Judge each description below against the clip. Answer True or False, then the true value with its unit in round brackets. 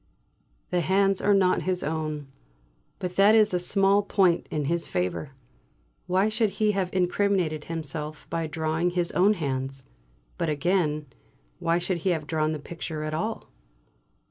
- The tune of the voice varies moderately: True (4.0 semitones)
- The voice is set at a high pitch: False (170 Hz)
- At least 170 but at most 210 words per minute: False (155 wpm)